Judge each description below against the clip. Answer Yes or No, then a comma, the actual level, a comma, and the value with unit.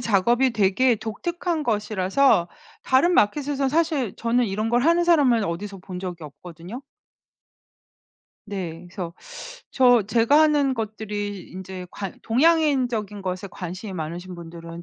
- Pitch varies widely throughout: Yes, wide, 6.1 semitones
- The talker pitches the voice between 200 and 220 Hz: Yes, high, 215 Hz